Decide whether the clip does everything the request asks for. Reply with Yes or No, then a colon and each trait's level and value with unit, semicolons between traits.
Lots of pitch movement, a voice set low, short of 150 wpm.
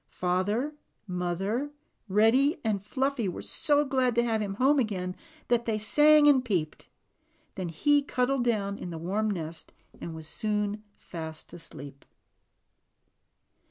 No: wide, 6.0 semitones; high, 215 Hz; slow, 135 wpm